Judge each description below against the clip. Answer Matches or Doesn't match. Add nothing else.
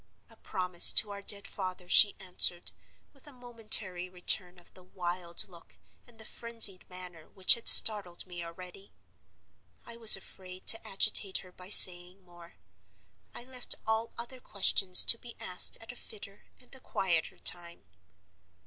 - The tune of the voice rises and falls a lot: Doesn't match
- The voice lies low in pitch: Doesn't match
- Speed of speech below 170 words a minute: Matches